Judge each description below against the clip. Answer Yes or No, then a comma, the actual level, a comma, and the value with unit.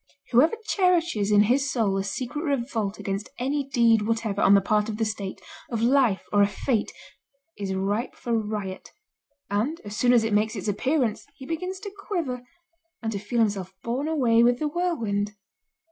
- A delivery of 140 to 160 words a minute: No, average, 180 wpm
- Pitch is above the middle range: Yes, high, 230 Hz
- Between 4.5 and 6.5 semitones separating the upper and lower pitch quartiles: Yes, average, 5.0 semitones